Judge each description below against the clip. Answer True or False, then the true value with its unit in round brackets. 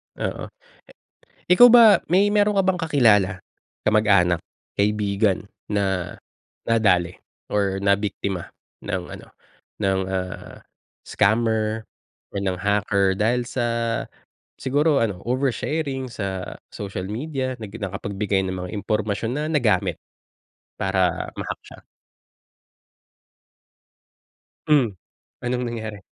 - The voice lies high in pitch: False (105 Hz)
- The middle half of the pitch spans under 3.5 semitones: False (4.5 semitones)